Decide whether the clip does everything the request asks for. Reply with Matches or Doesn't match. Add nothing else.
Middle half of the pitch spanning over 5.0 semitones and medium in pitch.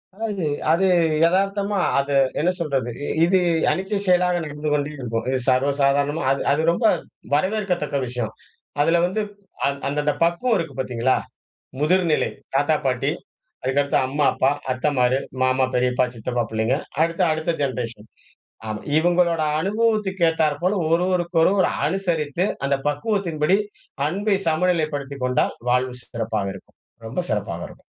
Matches